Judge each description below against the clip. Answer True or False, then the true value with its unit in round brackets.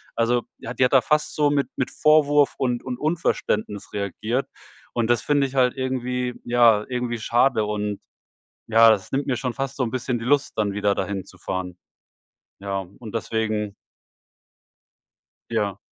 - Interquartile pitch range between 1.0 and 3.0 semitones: False (3.8 semitones)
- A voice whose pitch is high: False (120 Hz)